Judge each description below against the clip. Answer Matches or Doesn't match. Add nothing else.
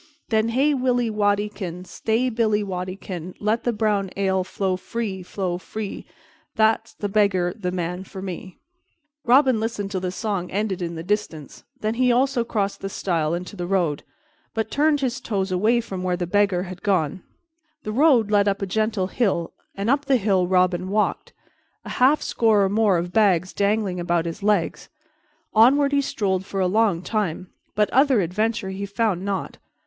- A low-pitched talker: Doesn't match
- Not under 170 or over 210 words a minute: Matches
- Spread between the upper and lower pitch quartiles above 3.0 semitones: Matches